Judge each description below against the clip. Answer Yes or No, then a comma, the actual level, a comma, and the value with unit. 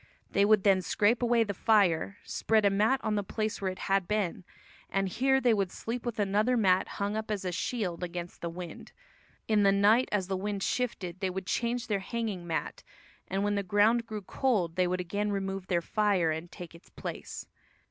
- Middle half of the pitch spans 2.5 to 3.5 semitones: Yes, average, 2.9 semitones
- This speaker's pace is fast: Yes, fast, 210 wpm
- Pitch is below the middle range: No, high, 200 Hz